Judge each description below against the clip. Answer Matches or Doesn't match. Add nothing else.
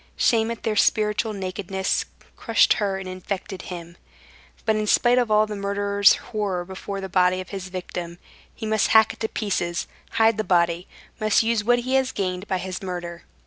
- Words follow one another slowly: Doesn't match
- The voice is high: Matches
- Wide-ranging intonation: Doesn't match